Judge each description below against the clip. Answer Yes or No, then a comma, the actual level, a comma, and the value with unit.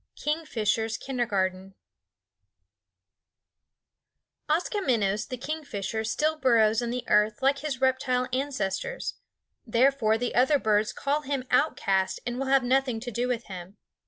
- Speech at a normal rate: No, slow, 125 wpm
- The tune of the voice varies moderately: Yes, average, 4.0 semitones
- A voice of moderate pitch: No, very high, 250 Hz